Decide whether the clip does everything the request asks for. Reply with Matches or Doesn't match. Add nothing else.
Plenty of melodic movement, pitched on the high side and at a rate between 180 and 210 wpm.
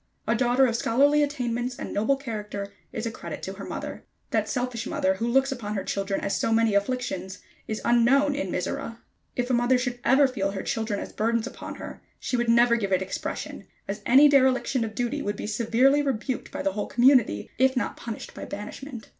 Doesn't match